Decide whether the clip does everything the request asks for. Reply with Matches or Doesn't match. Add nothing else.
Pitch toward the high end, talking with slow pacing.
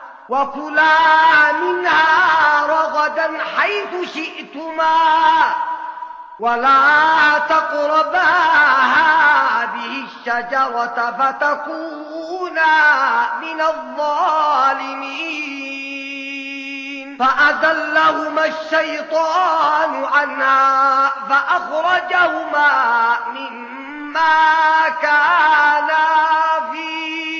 Matches